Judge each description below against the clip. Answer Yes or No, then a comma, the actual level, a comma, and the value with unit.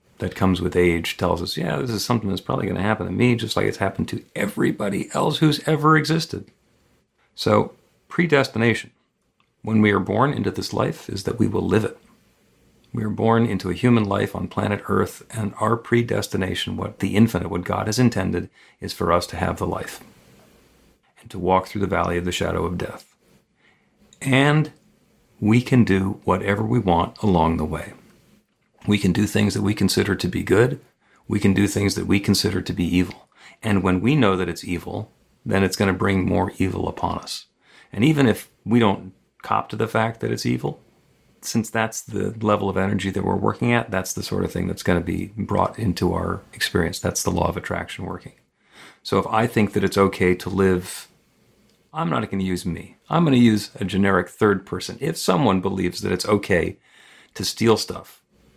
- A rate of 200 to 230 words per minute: Yes, fast, 205 wpm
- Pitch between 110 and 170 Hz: No, low, 100 Hz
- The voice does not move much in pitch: No, average, 3.5 semitones